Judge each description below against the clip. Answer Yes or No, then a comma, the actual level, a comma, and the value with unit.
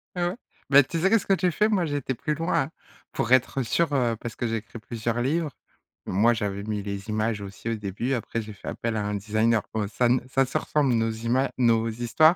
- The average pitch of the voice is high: No, low, 120 Hz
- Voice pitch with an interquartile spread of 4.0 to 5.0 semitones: Yes, average, 4.4 semitones